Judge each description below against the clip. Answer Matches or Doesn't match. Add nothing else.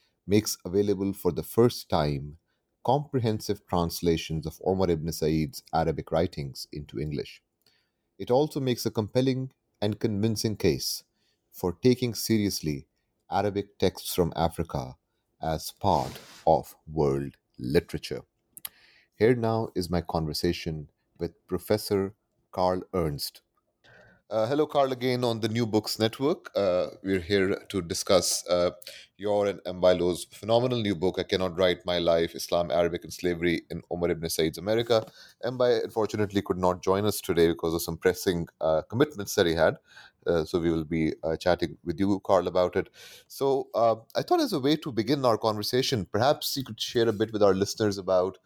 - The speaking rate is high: Doesn't match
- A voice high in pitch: Doesn't match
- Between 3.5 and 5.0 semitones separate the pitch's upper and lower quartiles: Matches